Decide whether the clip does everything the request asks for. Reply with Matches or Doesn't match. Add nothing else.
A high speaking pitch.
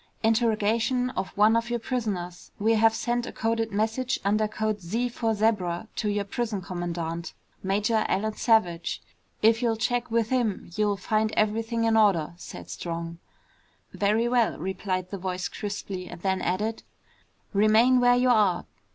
Matches